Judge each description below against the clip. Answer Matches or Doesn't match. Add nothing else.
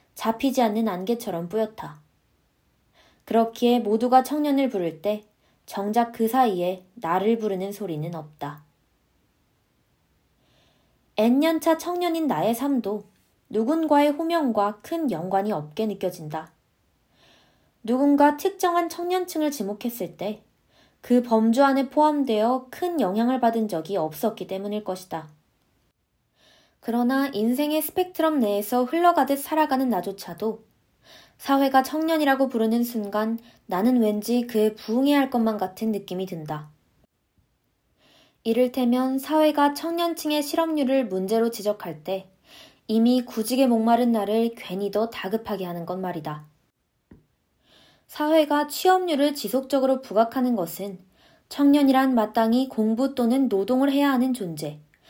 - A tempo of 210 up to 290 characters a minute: Matches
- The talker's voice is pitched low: Doesn't match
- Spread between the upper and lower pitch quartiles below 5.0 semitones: Doesn't match